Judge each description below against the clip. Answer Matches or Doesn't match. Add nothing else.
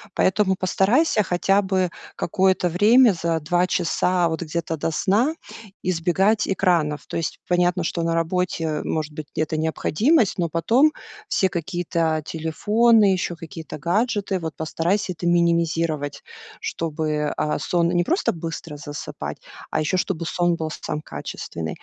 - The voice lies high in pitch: Doesn't match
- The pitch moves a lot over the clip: Doesn't match